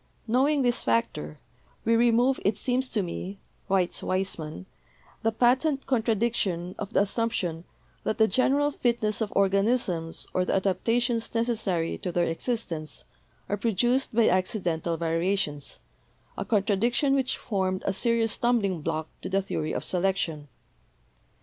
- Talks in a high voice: Yes, high, 205 Hz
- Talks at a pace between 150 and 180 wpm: No, slow, 135 wpm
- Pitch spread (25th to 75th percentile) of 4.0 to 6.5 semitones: Yes, average, 4.9 semitones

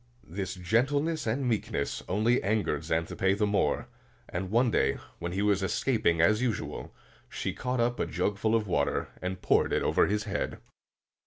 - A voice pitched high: No, low, 105 Hz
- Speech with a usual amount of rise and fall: Yes, average, 4.2 semitones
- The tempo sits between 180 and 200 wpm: No, average, 170 wpm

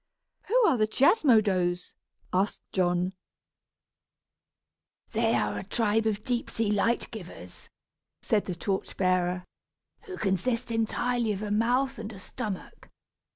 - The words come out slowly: Yes, slow, 125 wpm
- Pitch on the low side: No, high, 215 Hz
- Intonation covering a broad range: No, average, 4.0 semitones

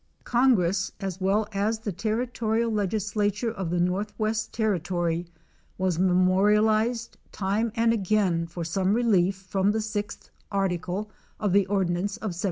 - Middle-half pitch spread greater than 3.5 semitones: No, average, 2.8 semitones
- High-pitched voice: Yes, high, 200 Hz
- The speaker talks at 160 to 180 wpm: No, average, 140 wpm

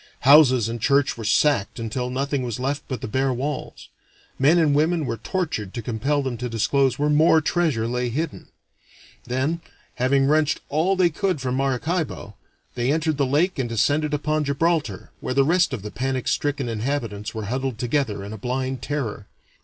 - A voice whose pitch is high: No, low, 135 Hz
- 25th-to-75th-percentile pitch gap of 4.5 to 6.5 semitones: No, average, 3.8 semitones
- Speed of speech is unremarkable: Yes, average, 185 wpm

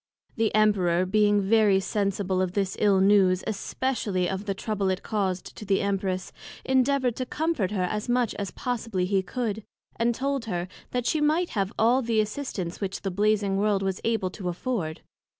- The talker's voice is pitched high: Yes, high, 205 Hz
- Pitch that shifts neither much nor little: Yes, average, 3.2 semitones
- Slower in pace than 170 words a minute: No, average, 180 wpm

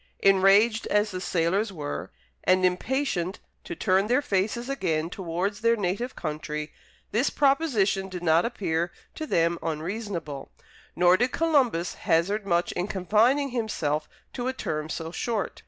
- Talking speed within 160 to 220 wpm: No, average, 140 wpm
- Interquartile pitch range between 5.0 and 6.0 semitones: Yes, average, 5.3 semitones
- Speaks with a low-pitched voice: No, high, 190 Hz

